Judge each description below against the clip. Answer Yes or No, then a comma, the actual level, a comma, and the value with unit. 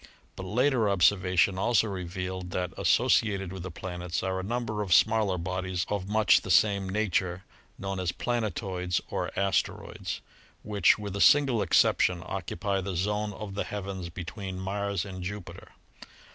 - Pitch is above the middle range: No, very low, 95 Hz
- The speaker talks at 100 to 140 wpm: No, average, 155 wpm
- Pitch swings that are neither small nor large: No, narrow, 2.1 semitones